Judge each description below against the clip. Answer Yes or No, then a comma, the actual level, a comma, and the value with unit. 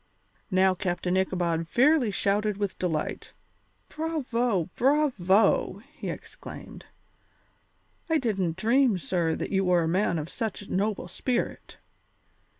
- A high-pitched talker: Yes, high, 195 Hz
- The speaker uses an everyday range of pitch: Yes, average, 4.8 semitones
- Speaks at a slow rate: Yes, slow, 120 wpm